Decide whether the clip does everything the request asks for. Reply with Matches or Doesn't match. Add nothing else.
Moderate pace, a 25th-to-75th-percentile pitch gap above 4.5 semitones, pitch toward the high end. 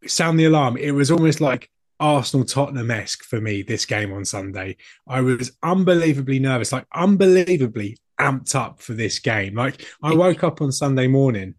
Doesn't match